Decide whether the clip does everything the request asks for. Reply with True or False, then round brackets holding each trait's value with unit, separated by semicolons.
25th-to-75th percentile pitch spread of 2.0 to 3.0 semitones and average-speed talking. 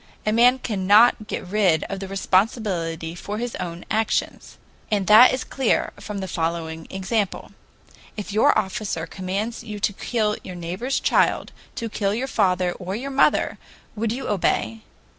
False (3.5 semitones; 160 wpm)